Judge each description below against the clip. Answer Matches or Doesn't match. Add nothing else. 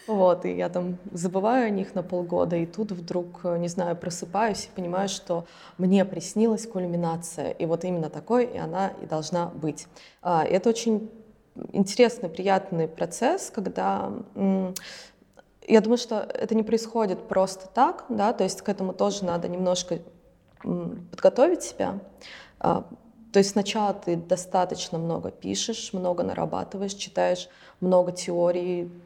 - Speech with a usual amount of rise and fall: Matches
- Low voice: Doesn't match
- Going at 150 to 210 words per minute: Doesn't match